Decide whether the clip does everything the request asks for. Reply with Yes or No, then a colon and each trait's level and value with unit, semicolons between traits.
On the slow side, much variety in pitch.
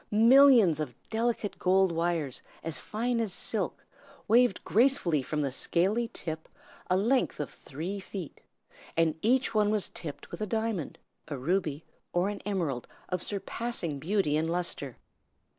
No: average, 145 wpm; wide, 5.7 semitones